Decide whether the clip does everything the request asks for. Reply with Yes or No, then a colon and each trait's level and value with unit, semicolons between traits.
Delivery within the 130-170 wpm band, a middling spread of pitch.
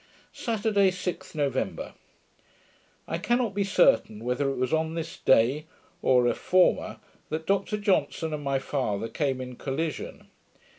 No: average, 140 wpm; wide, 6.3 semitones